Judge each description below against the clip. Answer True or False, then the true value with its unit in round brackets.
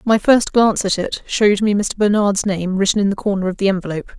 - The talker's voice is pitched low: False (200 Hz)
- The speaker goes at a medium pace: False (245 wpm)